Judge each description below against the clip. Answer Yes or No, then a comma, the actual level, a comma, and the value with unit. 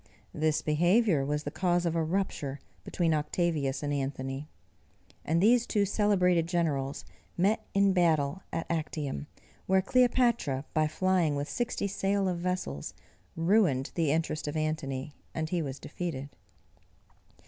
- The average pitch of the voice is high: No, medium, 165 Hz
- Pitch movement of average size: Yes, average, 4.4 semitones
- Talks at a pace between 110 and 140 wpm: Yes, slow, 135 wpm